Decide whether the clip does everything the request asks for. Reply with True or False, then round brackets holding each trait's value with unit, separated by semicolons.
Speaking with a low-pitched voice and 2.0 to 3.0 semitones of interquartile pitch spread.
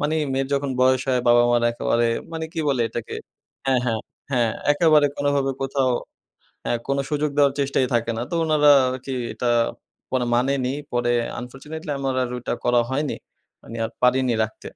True (130 Hz; 2.7 semitones)